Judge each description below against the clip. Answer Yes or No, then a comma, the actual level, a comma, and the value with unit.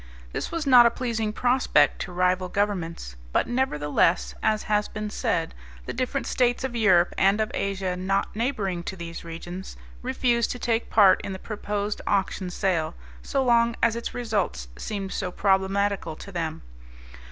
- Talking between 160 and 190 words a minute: Yes, average, 165 wpm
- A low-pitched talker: No, high, 200 Hz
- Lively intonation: No, average, 4.3 semitones